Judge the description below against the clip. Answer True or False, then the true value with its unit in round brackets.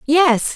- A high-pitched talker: True (300 Hz)